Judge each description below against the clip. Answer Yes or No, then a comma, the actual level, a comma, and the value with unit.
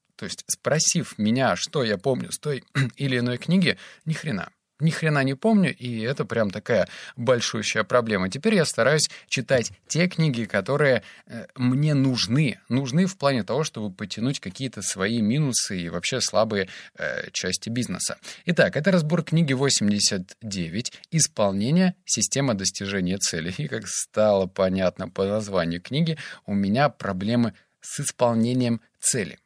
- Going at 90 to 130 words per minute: No, average, 145 wpm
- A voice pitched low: Yes, low, 120 Hz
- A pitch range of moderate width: No, wide, 6.3 semitones